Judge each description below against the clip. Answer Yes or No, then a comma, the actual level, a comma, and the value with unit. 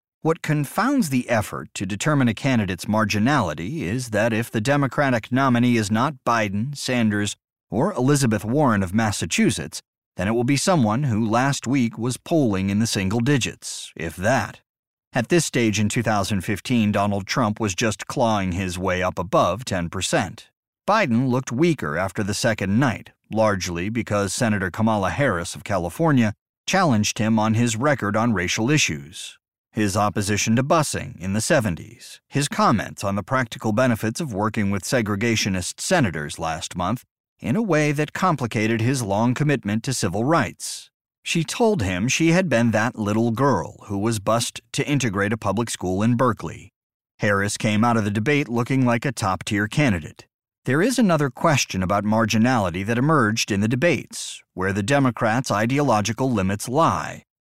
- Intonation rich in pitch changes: No, average, 4.1 semitones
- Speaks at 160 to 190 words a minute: Yes, average, 165 wpm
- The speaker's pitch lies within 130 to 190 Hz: No, low, 115 Hz